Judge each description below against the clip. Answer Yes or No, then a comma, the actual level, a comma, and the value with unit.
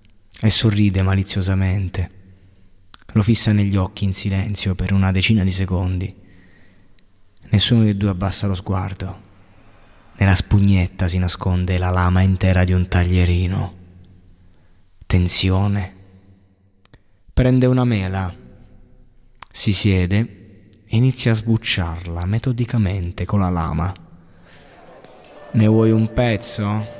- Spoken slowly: Yes, slow, 105 wpm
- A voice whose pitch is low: Yes, very low, 95 Hz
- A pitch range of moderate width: No, narrow, 2.2 semitones